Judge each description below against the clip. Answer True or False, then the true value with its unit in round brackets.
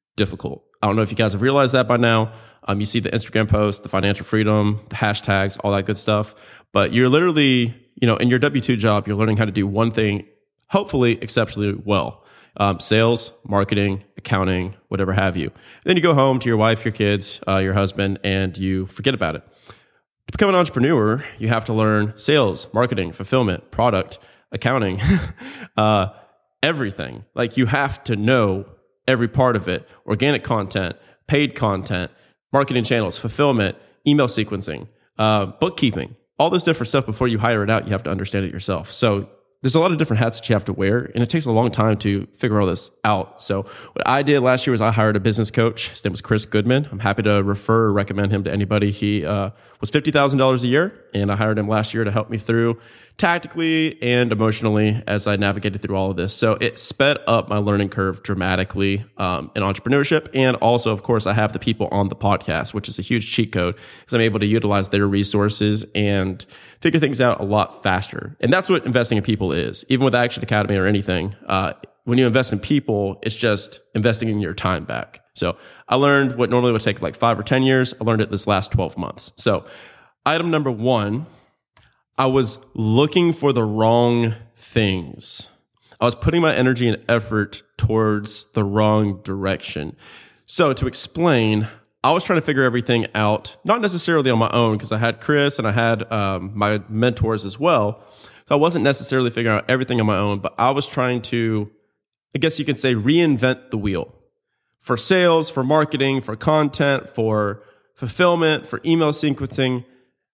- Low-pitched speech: True (110 Hz)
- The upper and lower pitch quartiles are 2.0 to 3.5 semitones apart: False (4.0 semitones)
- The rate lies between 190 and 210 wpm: True (200 wpm)